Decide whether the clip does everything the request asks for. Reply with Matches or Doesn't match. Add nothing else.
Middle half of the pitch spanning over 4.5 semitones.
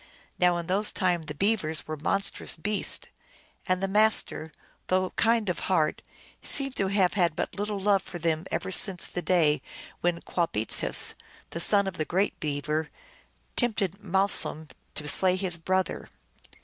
Doesn't match